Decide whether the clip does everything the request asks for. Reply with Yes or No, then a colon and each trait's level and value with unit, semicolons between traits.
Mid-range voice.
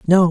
Yes: medium, 175 Hz